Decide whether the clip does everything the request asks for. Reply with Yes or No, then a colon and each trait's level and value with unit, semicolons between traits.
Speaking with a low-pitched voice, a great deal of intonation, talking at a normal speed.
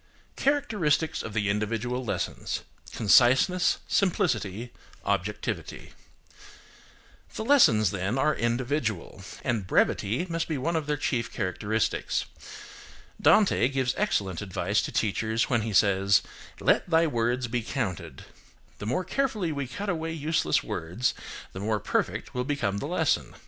No: low, 120 Hz; wide, 7.3 semitones; slow, 130 wpm